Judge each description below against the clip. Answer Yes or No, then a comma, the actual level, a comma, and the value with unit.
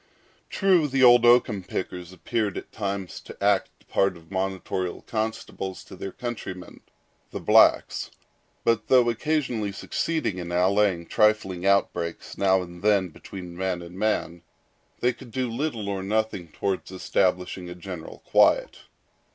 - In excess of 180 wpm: No, average, 140 wpm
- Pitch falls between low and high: No, low, 100 Hz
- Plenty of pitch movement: No, average, 3.8 semitones